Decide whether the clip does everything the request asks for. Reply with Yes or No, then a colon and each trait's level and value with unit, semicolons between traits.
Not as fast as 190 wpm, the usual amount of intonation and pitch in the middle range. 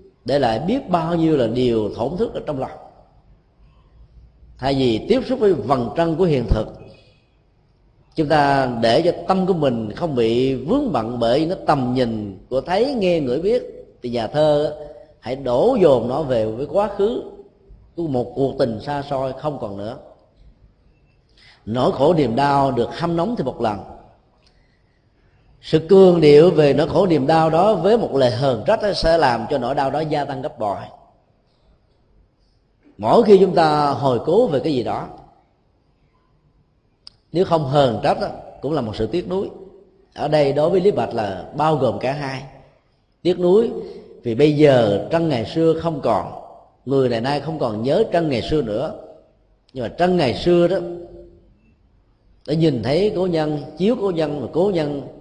No: average, 180 wpm; wide, 6.1 semitones; medium, 150 Hz